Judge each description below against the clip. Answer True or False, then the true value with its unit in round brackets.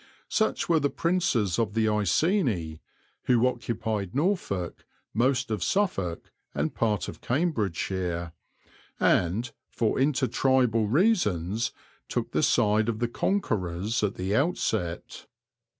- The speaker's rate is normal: False (120 wpm)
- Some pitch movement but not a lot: False (6.0 semitones)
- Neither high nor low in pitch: False (110 Hz)